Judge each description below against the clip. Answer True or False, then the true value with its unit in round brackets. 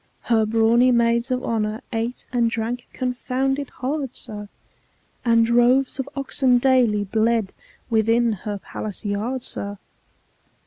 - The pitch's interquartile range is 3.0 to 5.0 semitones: False (2.4 semitones)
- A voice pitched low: False (235 Hz)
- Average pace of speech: False (125 wpm)